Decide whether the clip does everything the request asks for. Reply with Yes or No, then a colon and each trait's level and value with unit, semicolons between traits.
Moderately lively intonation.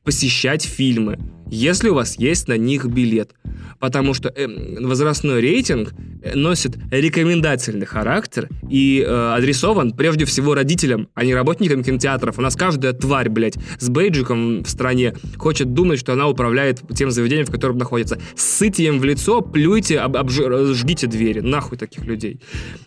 Yes: average, 3.1 semitones